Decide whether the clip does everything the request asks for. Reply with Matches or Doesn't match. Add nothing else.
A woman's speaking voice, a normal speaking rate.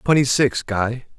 Doesn't match